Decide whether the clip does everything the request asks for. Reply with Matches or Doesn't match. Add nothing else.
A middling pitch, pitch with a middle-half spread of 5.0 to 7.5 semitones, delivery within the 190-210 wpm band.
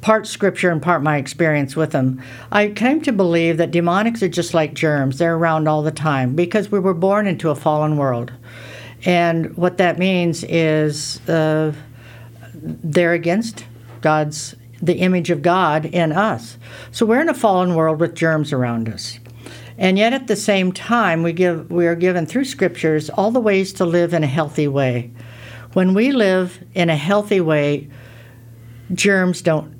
Doesn't match